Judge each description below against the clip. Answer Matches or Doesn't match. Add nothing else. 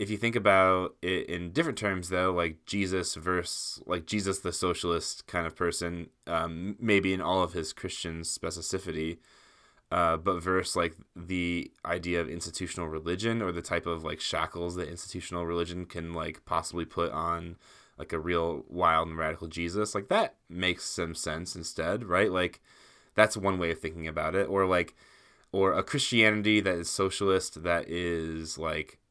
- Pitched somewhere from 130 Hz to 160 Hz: Doesn't match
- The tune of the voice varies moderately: Doesn't match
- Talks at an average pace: Matches